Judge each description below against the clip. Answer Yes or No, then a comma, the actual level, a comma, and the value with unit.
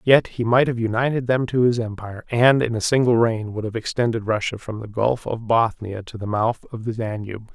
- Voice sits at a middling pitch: No, low, 115 Hz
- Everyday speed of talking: No, fast, 230 wpm